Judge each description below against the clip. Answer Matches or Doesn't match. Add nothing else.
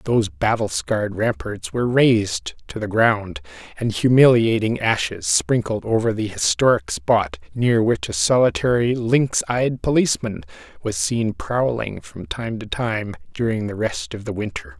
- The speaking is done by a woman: Doesn't match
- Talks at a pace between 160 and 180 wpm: Doesn't match